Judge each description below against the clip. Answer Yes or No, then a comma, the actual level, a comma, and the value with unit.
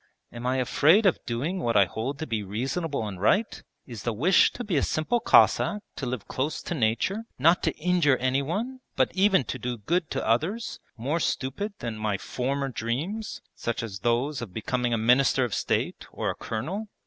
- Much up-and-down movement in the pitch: Yes, wide, 6.9 semitones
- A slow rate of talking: No, average, 195 wpm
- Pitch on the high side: No, low, 130 Hz